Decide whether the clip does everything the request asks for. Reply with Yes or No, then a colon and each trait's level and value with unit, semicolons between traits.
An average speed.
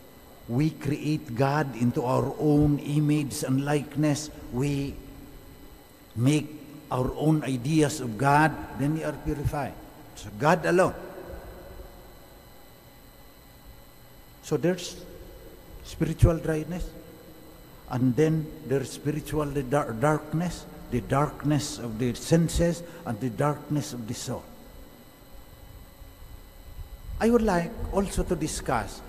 No: slow, 105 wpm